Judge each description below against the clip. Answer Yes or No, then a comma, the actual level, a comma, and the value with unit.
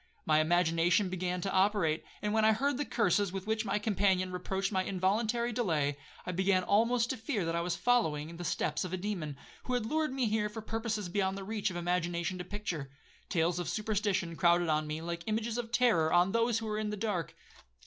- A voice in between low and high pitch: No, high, 195 Hz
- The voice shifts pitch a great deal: No, average, 4.0 semitones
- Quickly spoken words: Yes, fast, 215 wpm